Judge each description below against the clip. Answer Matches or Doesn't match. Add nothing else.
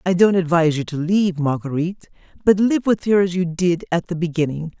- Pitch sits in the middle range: Matches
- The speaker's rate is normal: Doesn't match